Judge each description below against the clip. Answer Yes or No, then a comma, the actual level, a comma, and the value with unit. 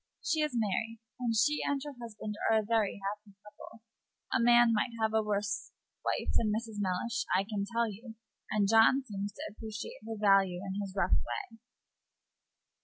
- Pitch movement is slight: Yes, narrow, 2.3 semitones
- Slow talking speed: No, average, 180 wpm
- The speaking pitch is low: No, high, 215 Hz